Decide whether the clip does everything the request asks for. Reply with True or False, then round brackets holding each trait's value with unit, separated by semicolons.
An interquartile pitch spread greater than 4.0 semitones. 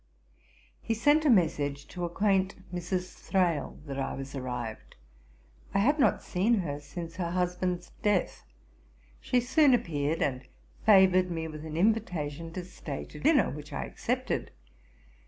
True (5.0 semitones)